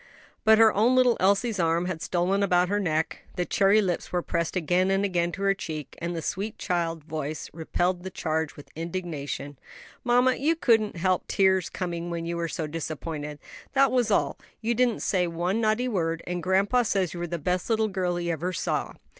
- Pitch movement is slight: No, average, 3.5 semitones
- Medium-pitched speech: Yes, medium, 180 Hz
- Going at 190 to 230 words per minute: Yes, fast, 205 wpm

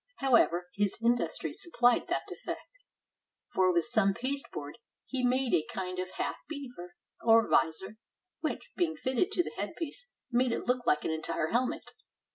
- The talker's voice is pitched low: No, high, 235 Hz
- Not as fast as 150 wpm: No, average, 155 wpm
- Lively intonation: Yes, wide, 6.1 semitones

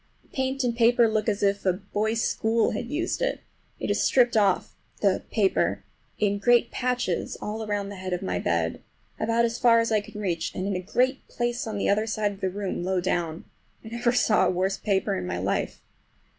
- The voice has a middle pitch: No, high, 210 Hz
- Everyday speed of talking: No, fast, 210 wpm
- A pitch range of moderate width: Yes, average, 3.5 semitones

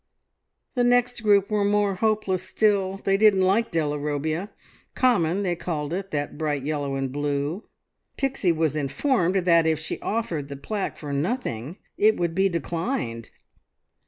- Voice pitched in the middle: Yes, medium, 175 Hz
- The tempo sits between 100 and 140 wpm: No, average, 155 wpm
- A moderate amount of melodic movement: No, wide, 5.8 semitones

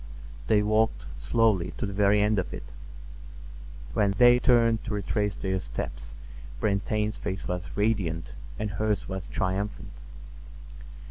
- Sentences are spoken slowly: Yes, slow, 130 wpm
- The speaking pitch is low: Yes, low, 105 Hz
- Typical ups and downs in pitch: No, narrow, 2.0 semitones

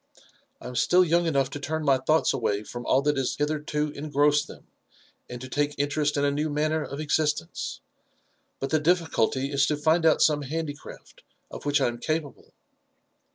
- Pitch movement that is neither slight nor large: No, narrow, 2.0 semitones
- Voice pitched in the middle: Yes, medium, 145 Hz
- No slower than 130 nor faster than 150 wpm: No, average, 185 wpm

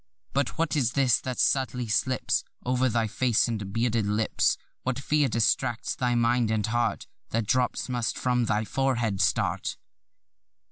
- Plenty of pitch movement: No, narrow, 2.5 semitones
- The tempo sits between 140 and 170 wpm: Yes, average, 150 wpm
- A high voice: No, low, 120 Hz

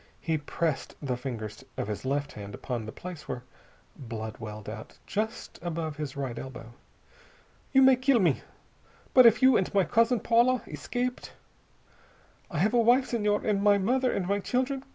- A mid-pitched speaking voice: Yes, medium, 180 Hz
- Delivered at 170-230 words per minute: Yes, average, 175 wpm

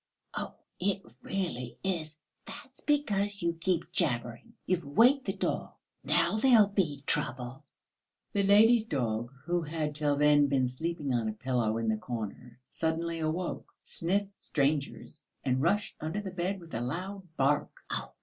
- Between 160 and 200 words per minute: No, average, 150 wpm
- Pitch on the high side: No, medium, 160 Hz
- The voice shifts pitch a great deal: Yes, wide, 6.7 semitones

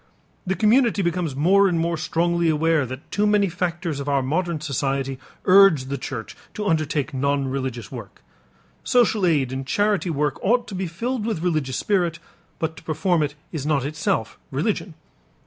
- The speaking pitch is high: No, medium, 160 Hz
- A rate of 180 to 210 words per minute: No, average, 170 wpm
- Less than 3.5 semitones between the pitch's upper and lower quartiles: No, average, 5.0 semitones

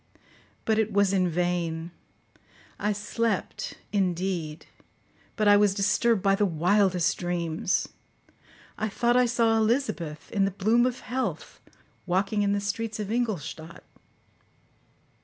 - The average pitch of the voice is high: Yes, high, 200 Hz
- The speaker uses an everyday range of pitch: Yes, average, 3.7 semitones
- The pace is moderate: No, slow, 125 wpm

